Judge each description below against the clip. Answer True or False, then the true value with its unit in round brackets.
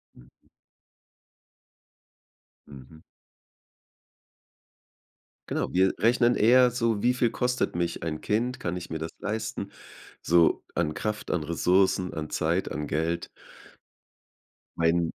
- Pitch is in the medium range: False (90 Hz)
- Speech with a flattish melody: False (5.8 semitones)